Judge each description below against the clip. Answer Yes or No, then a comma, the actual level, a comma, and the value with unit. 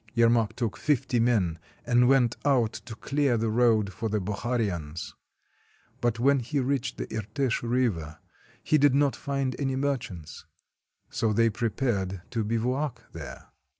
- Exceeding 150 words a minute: No, average, 145 wpm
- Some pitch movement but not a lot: Yes, average, 3.5 semitones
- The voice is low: Yes, low, 115 Hz